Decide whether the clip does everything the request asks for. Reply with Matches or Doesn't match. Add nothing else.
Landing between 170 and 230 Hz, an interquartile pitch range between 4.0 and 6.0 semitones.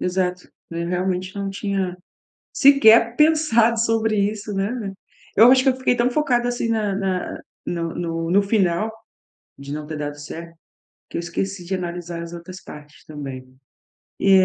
Matches